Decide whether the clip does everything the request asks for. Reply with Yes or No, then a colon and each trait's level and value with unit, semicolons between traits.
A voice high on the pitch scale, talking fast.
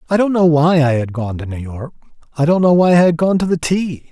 No: medium, 155 Hz; fast, 290 wpm